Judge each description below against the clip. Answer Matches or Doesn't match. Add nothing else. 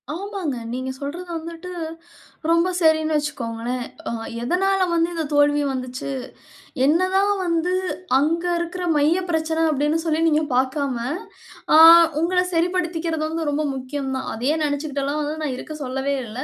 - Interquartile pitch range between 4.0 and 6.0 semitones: Doesn't match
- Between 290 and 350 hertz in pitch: Matches